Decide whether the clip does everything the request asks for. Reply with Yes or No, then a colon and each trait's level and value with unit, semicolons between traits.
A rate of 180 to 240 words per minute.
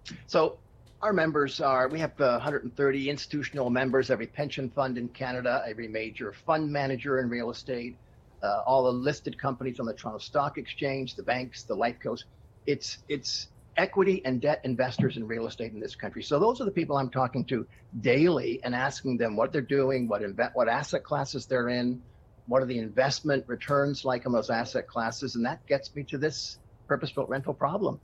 Yes: average, 195 wpm